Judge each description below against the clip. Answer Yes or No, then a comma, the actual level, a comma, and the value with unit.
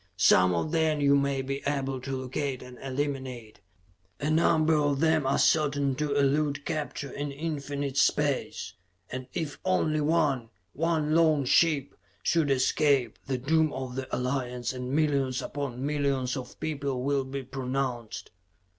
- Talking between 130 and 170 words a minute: Yes, average, 145 wpm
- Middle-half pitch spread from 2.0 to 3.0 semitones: Yes, narrow, 2.4 semitones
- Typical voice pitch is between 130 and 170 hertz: Yes, medium, 140 Hz